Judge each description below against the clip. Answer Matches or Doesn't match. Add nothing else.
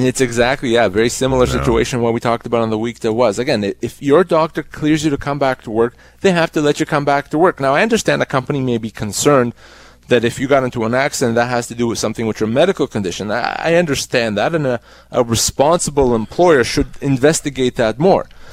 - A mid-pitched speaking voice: Doesn't match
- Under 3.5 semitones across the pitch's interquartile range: Doesn't match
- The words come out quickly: Matches